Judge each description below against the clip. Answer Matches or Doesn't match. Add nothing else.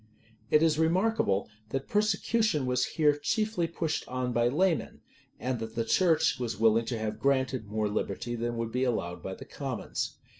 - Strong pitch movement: Matches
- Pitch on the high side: Doesn't match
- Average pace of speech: Matches